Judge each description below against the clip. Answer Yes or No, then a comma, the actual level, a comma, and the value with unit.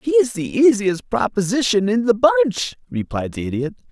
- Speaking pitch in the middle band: No, high, 210 Hz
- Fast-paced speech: No, average, 155 wpm